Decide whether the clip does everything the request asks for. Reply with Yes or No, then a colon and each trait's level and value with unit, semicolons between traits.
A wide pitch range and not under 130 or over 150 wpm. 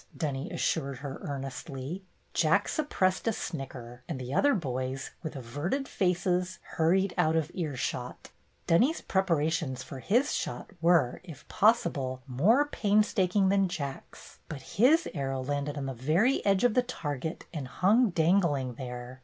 Yes: wide, 6.3 semitones; average, 145 wpm